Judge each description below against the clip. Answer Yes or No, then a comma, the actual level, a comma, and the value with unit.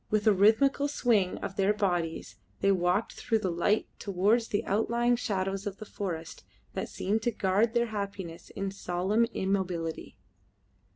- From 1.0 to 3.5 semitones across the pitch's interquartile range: Yes, average, 3.0 semitones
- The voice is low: No, high, 200 Hz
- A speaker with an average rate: Yes, average, 155 wpm